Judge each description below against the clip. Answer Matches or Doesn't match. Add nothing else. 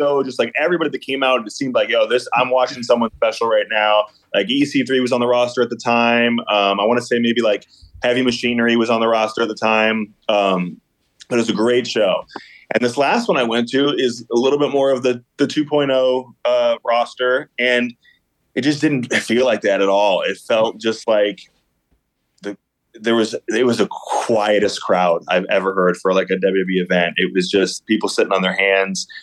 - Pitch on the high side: Doesn't match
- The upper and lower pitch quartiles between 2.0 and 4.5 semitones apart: Matches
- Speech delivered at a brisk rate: Matches